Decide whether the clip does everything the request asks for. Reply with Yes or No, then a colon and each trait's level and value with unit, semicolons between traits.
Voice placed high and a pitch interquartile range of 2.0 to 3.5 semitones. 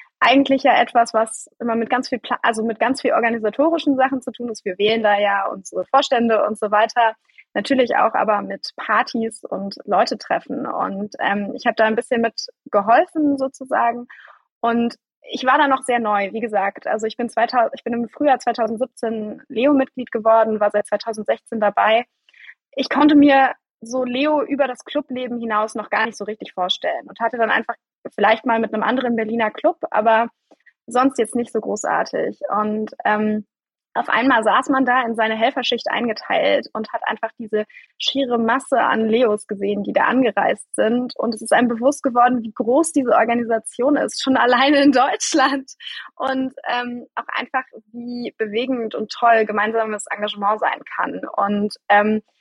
Yes: high, 235 Hz; average, 3.1 semitones